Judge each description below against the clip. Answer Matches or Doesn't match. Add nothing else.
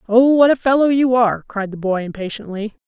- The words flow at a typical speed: Doesn't match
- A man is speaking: Doesn't match